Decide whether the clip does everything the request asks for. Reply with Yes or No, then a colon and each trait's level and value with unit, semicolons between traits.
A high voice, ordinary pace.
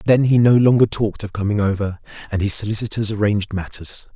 No: low, 105 Hz; average, 190 wpm